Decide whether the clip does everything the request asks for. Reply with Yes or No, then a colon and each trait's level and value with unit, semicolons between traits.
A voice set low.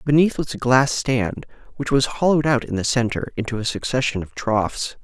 Yes: low, 125 Hz